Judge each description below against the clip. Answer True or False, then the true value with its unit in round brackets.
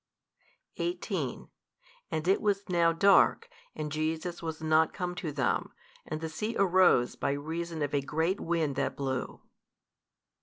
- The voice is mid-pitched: True (160 Hz)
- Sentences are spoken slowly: False (145 wpm)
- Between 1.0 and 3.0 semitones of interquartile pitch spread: True (2.7 semitones)